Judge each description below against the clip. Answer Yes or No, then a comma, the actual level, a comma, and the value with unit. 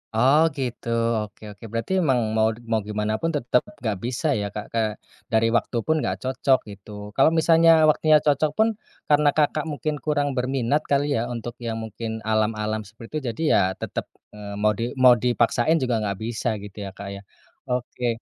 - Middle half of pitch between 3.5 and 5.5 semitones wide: Yes, average, 4.7 semitones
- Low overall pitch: Yes, low, 120 Hz